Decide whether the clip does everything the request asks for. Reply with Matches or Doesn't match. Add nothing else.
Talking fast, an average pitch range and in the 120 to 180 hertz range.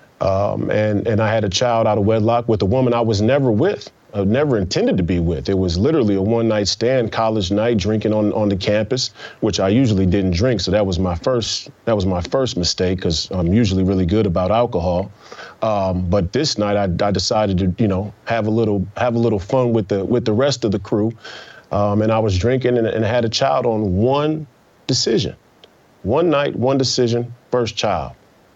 Doesn't match